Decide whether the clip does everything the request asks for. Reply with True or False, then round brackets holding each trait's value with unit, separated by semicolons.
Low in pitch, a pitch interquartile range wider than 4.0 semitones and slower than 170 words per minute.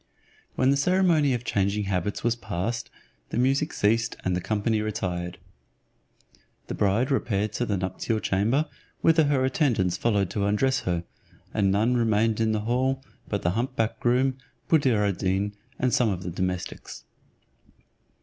True (110 Hz; 4.6 semitones; 160 wpm)